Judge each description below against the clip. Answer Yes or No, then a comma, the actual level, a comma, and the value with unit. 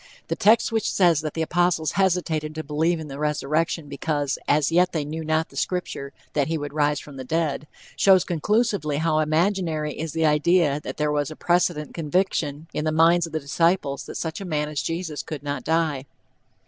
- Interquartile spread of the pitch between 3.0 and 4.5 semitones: No, narrow, 2.5 semitones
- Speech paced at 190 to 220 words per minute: Yes, average, 200 wpm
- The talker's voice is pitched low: No, medium, 155 Hz